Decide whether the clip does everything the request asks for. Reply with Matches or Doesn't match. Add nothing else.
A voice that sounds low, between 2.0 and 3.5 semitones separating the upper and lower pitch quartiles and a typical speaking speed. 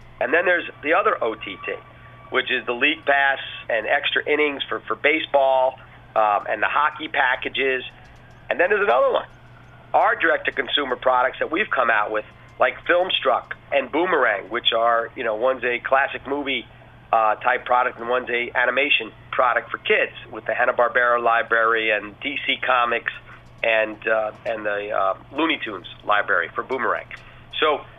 Matches